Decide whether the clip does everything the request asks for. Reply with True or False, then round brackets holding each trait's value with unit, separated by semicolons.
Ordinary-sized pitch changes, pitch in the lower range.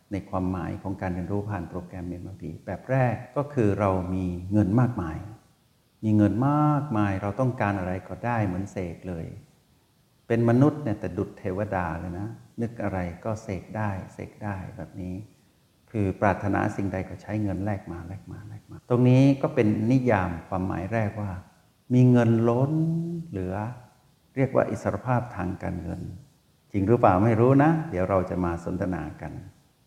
True (4.4 semitones; 105 Hz)